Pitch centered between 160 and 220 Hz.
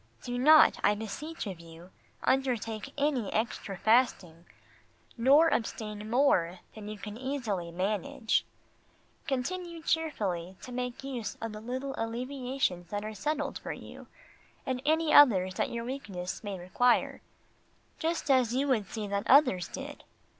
No: high, 230 Hz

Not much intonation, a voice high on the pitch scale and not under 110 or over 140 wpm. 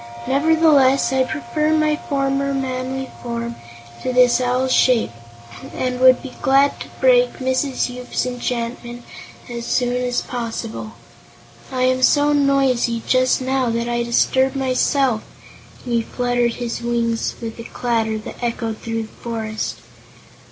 Yes: narrow, 2.1 semitones; very high, 250 Hz; slow, 135 wpm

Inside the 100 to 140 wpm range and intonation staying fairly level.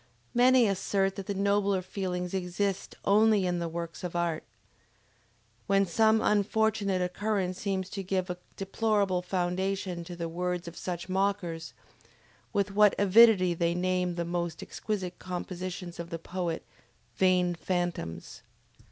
Yes: slow, 135 wpm; narrow, 2.2 semitones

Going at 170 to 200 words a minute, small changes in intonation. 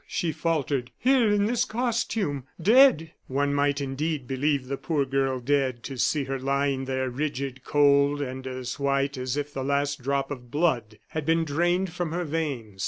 No: average, 175 wpm; average, 3.3 semitones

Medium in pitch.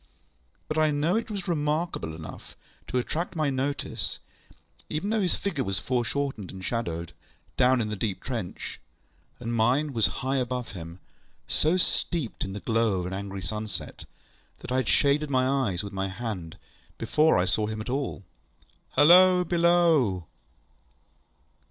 No: low, 125 Hz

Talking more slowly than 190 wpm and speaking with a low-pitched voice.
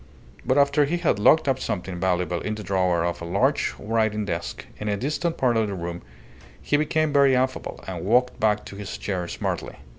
No: fast, 205 wpm; low, 105 Hz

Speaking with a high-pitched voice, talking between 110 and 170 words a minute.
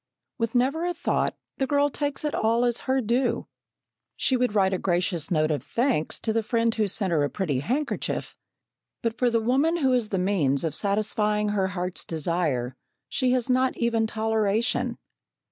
No: high, 220 Hz; average, 180 wpm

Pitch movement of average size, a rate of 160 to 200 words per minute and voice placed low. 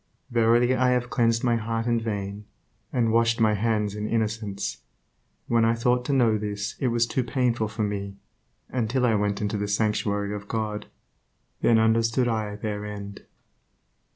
No: narrow, 2.1 semitones; average, 165 wpm; low, 110 Hz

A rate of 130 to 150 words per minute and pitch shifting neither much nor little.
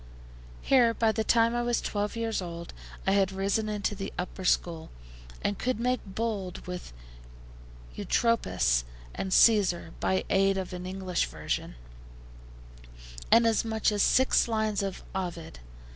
Yes: average, 145 wpm; average, 3.7 semitones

